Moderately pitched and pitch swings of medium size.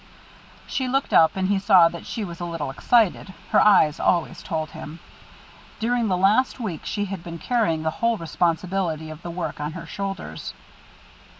Yes: medium, 180 Hz; average, 4.0 semitones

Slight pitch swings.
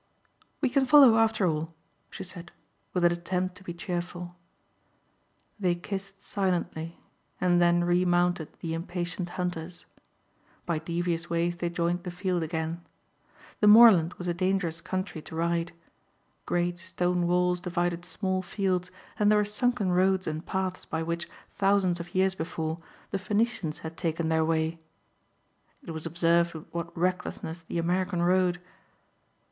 Yes: narrow, 1.8 semitones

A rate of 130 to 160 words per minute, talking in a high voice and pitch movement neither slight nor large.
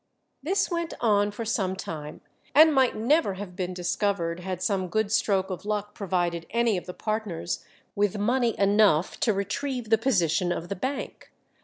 No: average, 170 wpm; high, 205 Hz; average, 3.9 semitones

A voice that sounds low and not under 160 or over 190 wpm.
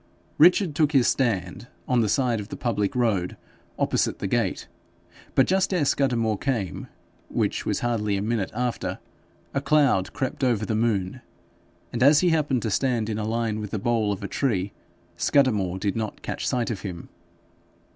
Yes: low, 115 Hz; average, 175 wpm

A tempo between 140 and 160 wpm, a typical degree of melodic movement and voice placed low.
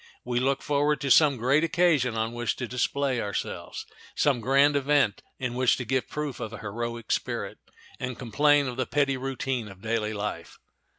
No: average, 180 wpm; average, 3.4 semitones; low, 130 Hz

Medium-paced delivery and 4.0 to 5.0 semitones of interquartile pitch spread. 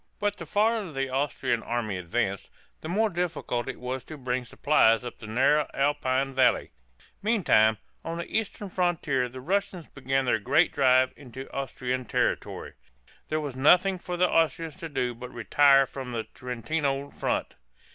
Yes: average, 160 wpm; average, 4.7 semitones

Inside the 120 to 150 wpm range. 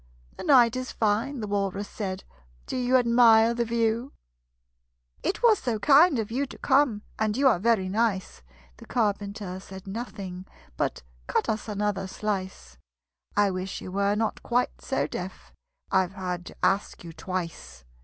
No: average, 160 wpm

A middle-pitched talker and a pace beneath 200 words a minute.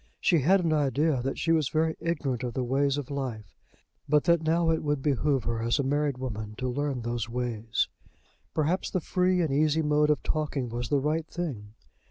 No: medium, 145 Hz; fast, 205 wpm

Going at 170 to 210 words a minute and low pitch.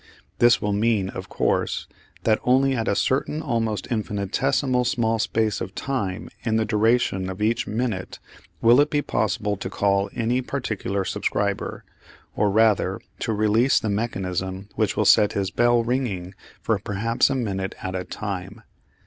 No: average, 155 wpm; low, 110 Hz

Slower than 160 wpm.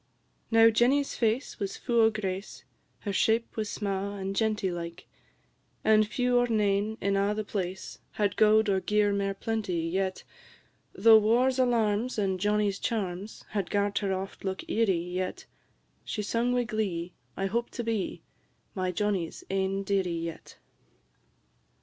Yes: average, 150 wpm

